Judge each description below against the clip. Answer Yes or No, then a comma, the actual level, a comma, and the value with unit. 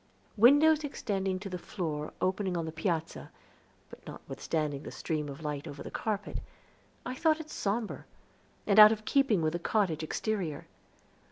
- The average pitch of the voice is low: No, high, 190 Hz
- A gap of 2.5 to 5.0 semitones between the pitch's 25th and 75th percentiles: No, wide, 5.5 semitones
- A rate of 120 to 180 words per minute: Yes, average, 160 wpm